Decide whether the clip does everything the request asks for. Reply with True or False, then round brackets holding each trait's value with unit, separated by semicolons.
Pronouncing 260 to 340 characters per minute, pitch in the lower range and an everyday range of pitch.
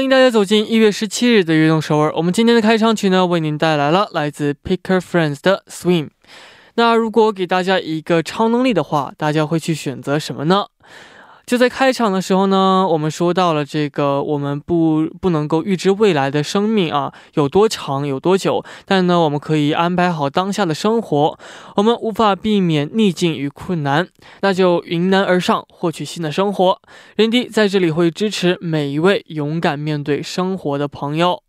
False (310 characters per minute; 180 Hz; 4.7 semitones)